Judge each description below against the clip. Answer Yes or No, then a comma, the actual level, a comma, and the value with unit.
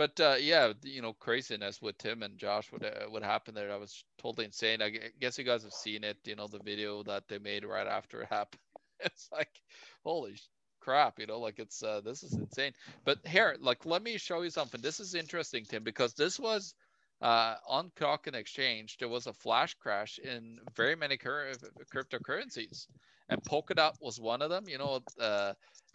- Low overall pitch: Yes, low, 120 Hz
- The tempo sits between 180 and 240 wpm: Yes, average, 200 wpm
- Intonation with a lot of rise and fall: Yes, wide, 6.7 semitones